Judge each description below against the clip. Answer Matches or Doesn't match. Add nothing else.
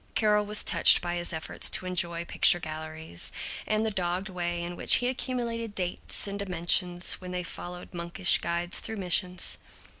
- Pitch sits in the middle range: Matches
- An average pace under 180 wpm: Matches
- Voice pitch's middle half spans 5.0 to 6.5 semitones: Doesn't match